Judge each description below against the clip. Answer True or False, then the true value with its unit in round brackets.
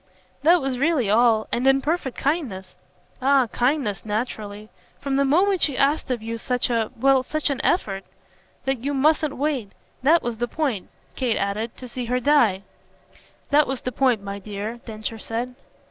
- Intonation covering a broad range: False (4.2 semitones)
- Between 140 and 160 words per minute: False (175 wpm)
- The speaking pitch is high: True (250 Hz)